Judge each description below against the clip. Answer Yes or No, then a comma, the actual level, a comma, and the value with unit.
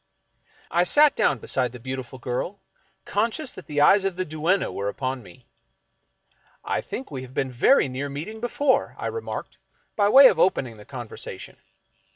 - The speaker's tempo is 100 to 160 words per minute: No, average, 180 wpm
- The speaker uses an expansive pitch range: Yes, wide, 7.9 semitones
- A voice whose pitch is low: No, medium, 145 Hz